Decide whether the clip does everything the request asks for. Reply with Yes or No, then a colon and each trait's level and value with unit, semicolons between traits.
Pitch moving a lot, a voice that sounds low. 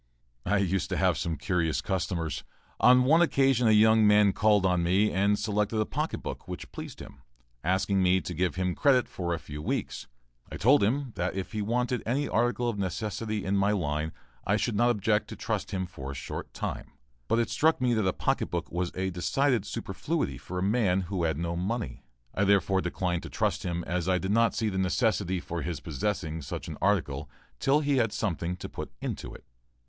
No: average, 4.2 semitones; low, 100 Hz